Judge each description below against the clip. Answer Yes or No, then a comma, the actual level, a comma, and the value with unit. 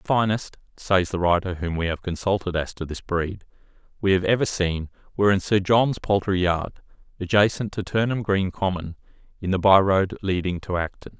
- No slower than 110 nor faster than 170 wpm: No, average, 180 wpm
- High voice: No, very low, 95 Hz